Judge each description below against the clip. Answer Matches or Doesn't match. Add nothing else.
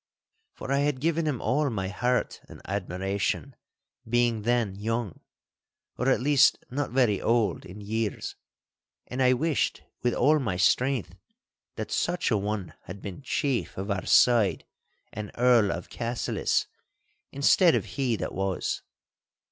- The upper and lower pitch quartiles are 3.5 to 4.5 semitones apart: Doesn't match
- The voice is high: Doesn't match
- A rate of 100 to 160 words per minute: Matches